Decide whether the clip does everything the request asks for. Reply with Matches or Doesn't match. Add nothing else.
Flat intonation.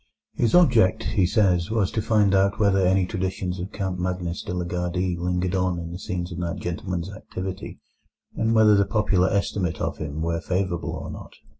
Matches